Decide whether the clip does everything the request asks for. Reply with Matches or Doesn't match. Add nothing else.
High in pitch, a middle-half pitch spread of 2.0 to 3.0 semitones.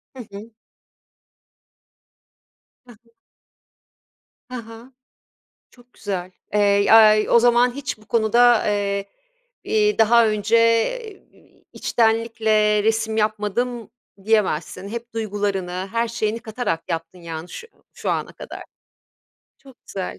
Matches